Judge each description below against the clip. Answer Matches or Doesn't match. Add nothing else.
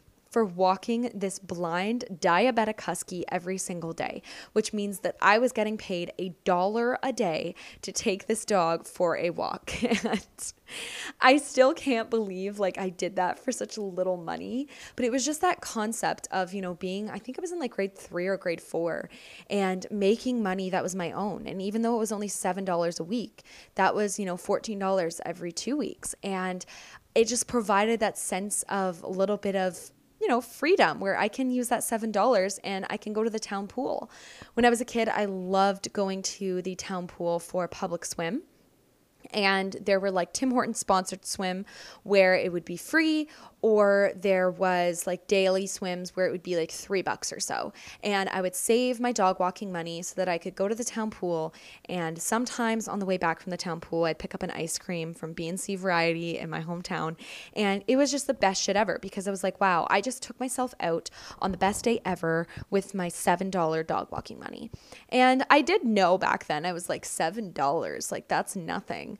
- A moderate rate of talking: Doesn't match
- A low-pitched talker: Doesn't match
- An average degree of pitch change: Matches